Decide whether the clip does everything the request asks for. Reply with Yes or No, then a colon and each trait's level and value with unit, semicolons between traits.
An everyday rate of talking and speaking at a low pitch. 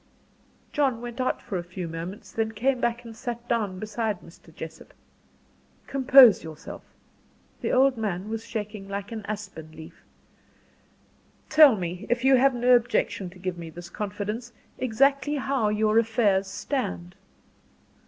No: average, 145 wpm; high, 220 Hz